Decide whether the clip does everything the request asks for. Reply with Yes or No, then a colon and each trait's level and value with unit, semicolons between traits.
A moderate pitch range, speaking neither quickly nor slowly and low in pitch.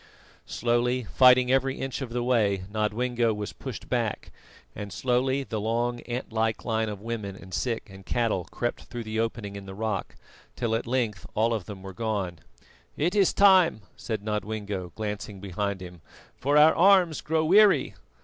Yes: average, 3.6 semitones; average, 170 wpm; low, 115 Hz